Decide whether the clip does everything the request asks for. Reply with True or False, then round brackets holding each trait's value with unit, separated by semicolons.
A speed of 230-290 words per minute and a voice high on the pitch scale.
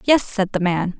True (240 wpm; 200 Hz)